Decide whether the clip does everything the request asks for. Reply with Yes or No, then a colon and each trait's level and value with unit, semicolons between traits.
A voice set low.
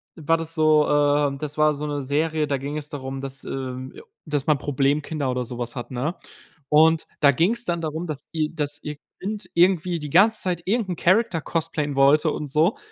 No: medium, 150 Hz